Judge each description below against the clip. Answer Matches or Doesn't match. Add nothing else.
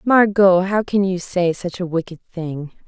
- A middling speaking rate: Matches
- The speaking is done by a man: Doesn't match